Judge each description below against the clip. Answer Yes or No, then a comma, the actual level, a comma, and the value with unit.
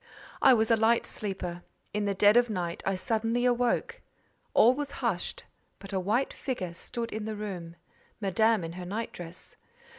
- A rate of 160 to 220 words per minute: Yes, average, 170 wpm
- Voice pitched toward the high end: Yes, high, 215 Hz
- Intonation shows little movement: No, average, 4.2 semitones